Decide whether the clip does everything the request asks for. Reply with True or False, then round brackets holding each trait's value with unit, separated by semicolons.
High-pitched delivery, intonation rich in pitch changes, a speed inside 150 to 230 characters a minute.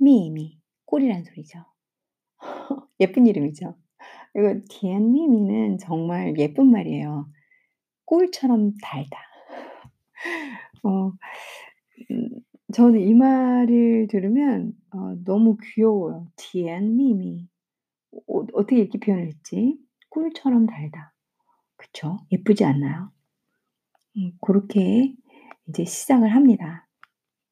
True (215 Hz; 5.9 semitones; 200 characters per minute)